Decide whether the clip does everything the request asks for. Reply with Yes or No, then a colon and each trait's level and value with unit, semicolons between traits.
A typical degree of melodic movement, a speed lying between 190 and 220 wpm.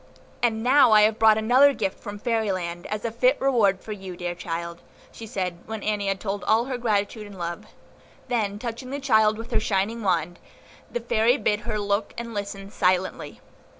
Yes: average, 3.1 semitones; average, 195 wpm